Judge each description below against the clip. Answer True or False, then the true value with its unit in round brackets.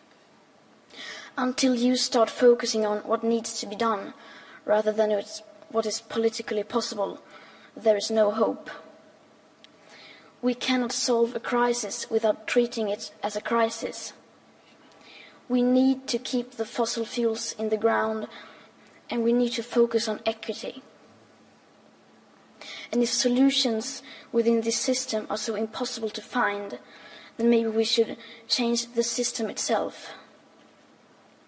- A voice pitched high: True (230 Hz)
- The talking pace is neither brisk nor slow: False (130 wpm)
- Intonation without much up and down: True (1.9 semitones)